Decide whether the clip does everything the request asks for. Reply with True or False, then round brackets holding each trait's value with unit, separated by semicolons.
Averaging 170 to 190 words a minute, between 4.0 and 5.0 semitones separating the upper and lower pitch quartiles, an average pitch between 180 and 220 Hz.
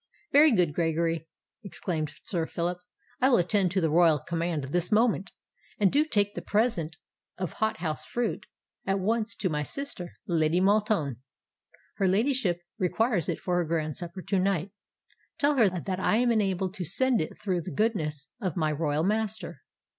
True (175 wpm; 4.5 semitones; 185 Hz)